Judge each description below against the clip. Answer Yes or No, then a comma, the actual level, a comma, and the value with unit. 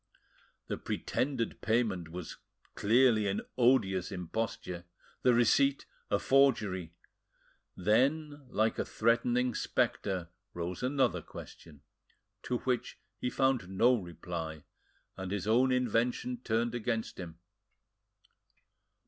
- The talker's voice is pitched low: Yes, low, 115 Hz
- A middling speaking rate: No, slow, 105 wpm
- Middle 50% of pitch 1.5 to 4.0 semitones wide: No, wide, 5.4 semitones